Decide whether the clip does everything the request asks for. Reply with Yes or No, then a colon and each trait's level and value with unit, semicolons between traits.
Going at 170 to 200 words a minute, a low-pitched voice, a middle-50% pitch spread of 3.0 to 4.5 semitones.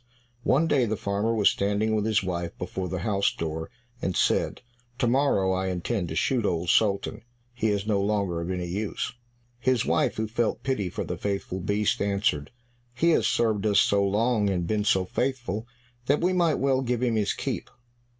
Yes: average, 190 wpm; low, 105 Hz; average, 3.9 semitones